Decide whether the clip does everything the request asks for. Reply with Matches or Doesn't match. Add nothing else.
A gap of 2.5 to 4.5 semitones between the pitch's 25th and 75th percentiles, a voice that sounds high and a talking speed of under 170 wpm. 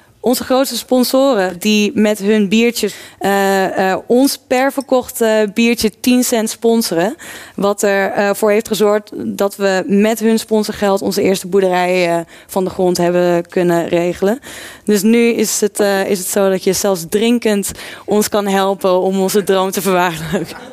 Matches